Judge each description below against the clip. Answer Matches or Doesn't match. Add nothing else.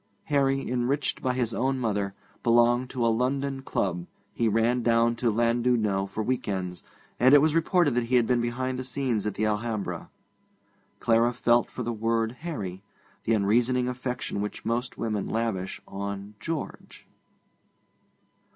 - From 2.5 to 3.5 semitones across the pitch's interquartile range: Matches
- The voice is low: Matches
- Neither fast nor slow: Matches